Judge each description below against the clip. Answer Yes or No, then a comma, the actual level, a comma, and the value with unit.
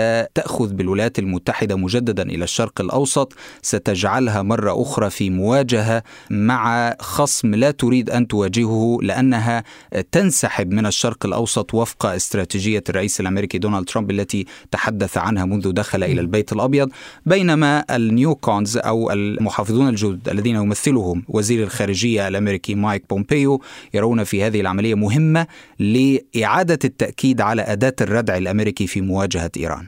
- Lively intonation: No, average, 3.4 semitones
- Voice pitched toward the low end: Yes, low, 110 Hz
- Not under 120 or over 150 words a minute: Yes, average, 130 wpm